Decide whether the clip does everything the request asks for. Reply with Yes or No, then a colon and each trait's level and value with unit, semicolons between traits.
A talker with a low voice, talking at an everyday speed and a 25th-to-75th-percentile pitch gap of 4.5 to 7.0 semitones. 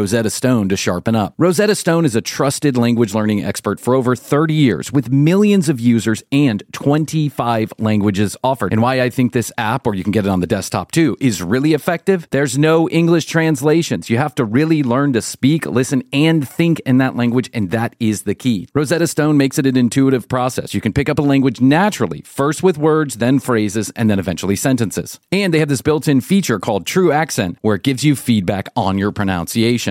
No: low, 130 Hz; fast, 215 wpm; average, 5.3 semitones